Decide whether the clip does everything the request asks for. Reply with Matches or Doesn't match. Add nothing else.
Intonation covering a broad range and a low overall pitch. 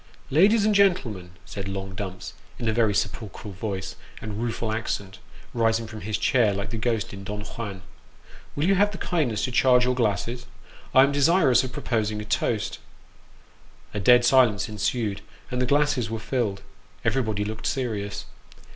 Doesn't match